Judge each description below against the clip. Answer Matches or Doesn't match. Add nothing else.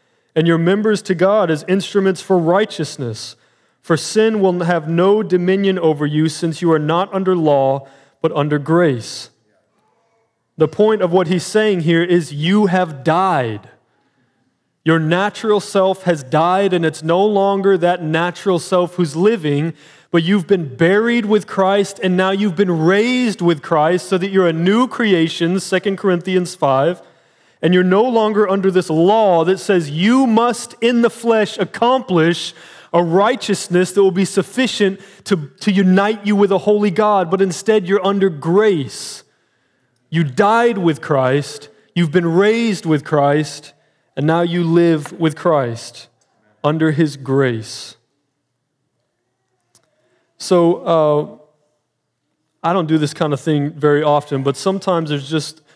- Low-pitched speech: Doesn't match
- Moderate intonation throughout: Matches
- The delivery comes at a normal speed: Matches